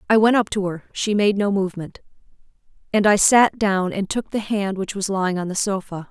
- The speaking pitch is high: Yes, high, 200 Hz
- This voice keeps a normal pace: No, fast, 225 wpm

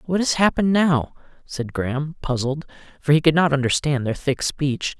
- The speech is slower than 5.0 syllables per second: No, 5.1 syllables/s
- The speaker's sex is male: Yes, male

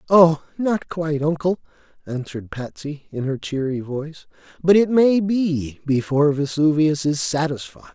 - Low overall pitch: No, medium, 155 Hz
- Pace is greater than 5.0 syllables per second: No, 4.7 syllables/s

